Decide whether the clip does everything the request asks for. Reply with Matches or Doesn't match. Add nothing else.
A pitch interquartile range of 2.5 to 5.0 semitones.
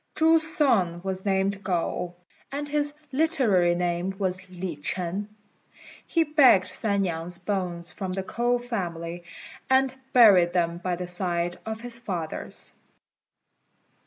Doesn't match